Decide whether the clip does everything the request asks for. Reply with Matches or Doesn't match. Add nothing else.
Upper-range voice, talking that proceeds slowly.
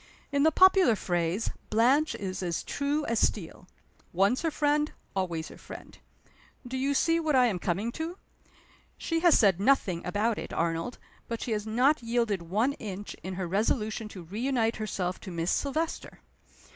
Doesn't match